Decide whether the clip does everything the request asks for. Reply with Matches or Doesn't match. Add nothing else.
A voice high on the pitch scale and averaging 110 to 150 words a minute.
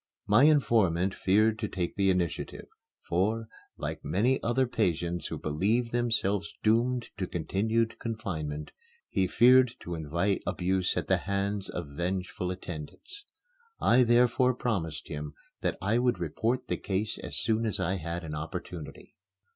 Doesn't match